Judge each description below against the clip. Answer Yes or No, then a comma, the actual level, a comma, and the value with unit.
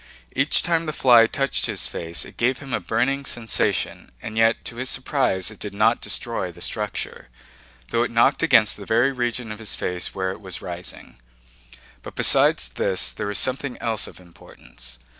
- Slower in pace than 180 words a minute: No, average, 185 wpm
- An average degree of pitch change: Yes, average, 4.6 semitones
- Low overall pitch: Yes, low, 115 Hz